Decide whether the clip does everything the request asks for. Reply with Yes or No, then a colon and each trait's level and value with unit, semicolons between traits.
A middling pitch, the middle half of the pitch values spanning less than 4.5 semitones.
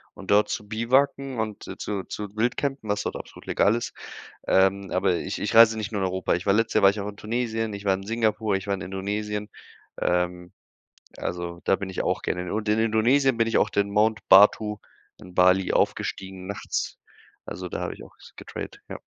No: low, 105 Hz; narrow, 2.5 semitones